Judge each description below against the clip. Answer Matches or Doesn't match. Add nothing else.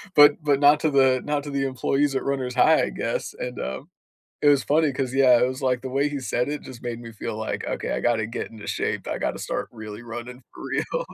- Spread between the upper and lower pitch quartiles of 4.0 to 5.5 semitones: Doesn't match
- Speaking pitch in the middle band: Doesn't match